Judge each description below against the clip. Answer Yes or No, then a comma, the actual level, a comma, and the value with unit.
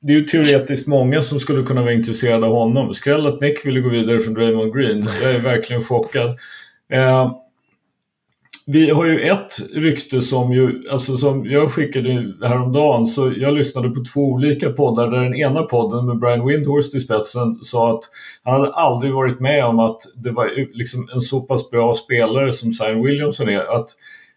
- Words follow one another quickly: No, average, 185 wpm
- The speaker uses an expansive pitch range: No, average, 3.2 semitones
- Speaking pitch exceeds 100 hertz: Yes, low, 130 Hz